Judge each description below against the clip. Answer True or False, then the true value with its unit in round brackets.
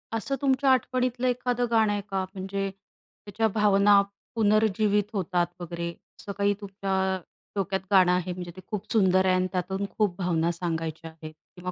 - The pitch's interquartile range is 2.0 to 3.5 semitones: True (2.9 semitones)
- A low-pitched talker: False (195 Hz)